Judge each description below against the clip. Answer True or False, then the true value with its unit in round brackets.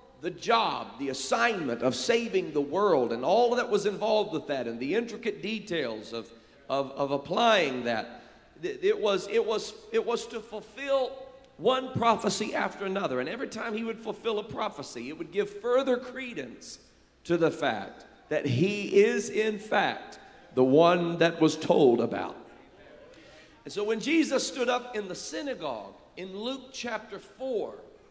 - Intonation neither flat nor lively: False (6.0 semitones)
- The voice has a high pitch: True (210 Hz)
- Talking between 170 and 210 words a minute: False (160 wpm)